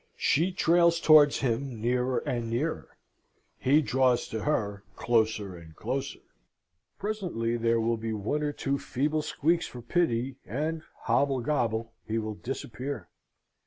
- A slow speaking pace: Yes, slow, 130 wpm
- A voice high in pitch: No, low, 125 Hz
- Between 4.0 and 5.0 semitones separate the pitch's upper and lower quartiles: Yes, average, 4.7 semitones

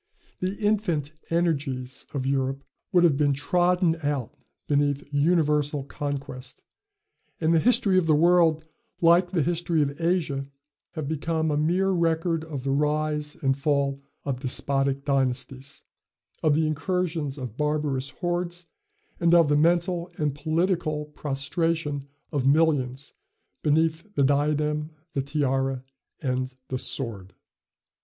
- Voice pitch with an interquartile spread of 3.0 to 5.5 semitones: Yes, average, 3.3 semitones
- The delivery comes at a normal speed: No, slow, 130 wpm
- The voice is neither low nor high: Yes, medium, 150 Hz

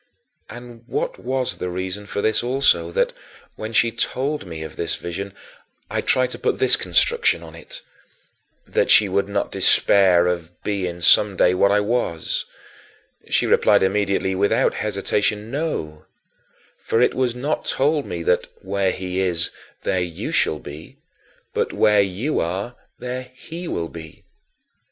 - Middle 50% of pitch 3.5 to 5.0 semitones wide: No, wide, 5.5 semitones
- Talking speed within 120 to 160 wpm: Yes, average, 155 wpm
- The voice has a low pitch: Yes, low, 100 Hz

